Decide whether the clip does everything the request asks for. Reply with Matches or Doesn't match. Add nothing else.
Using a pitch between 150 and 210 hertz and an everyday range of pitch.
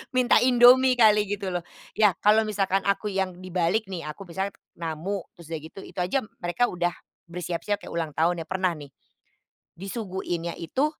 Matches